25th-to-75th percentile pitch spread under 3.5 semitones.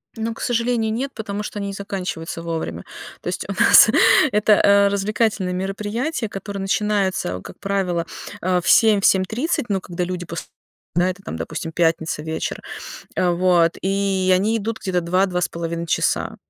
Yes: average, 3.0 semitones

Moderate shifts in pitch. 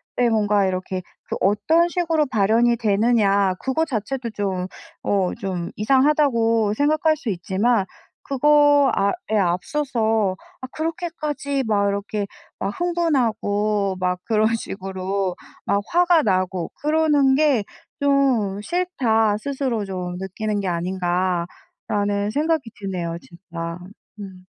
No: wide, 6.3 semitones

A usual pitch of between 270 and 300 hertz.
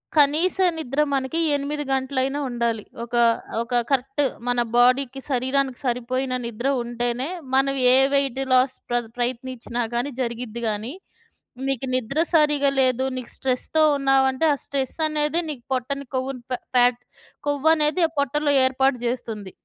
No: very high, 260 Hz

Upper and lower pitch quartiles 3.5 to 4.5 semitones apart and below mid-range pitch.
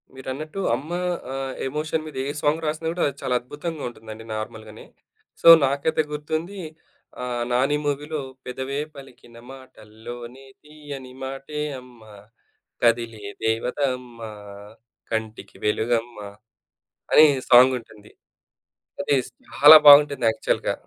Yes: average, 3.9 semitones; low, 130 Hz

